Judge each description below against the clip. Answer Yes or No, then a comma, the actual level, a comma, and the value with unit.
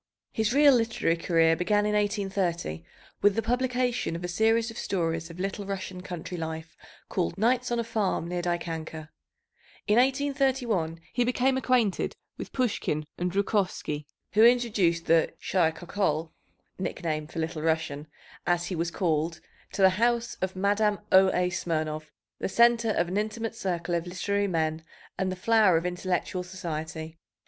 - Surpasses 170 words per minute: No, average, 155 wpm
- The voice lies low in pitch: No, medium, 185 Hz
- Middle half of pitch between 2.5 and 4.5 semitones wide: No, average, 5.0 semitones